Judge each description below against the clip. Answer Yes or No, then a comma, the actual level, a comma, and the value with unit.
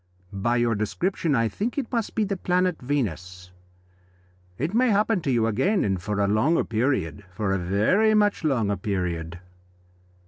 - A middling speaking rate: Yes, average, 165 wpm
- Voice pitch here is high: No, low, 120 Hz